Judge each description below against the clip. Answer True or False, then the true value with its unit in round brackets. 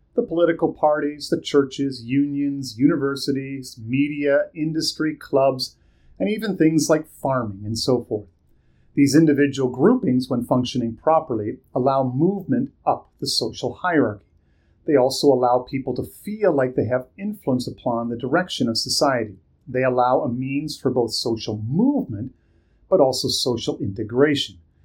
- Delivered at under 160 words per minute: True (140 wpm)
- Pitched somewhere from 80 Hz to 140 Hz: True (135 Hz)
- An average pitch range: True (3.6 semitones)